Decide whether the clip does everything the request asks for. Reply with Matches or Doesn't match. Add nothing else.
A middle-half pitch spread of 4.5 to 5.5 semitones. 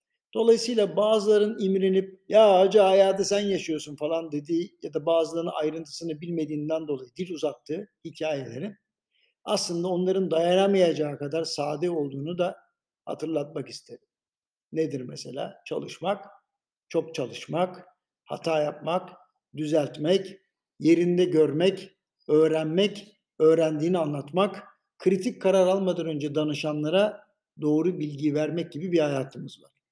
Doesn't match